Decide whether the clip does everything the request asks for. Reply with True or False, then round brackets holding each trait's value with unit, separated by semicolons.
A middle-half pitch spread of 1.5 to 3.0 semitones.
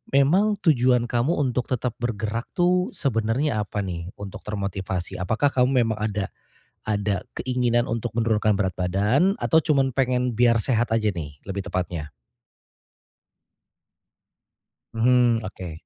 False (4.1 semitones)